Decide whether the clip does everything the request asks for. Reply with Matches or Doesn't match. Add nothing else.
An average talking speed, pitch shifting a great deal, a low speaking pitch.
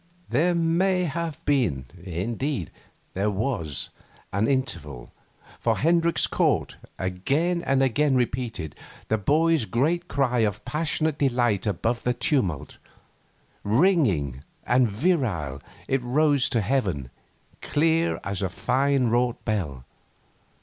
Doesn't match